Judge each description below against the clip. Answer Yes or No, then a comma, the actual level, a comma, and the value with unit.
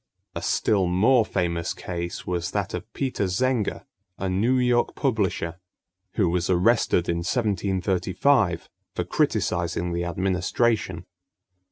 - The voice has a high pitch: No, very low, 95 Hz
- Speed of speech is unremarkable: No, slow, 120 wpm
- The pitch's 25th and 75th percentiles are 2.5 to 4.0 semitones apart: No, average, 4.4 semitones